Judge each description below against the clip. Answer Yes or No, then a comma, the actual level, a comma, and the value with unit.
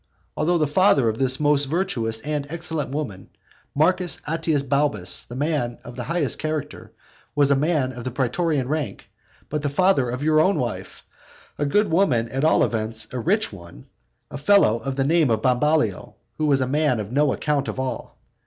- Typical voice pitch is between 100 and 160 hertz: Yes, medium, 140 Hz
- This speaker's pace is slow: No, average, 180 wpm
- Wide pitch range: No, average, 4.1 semitones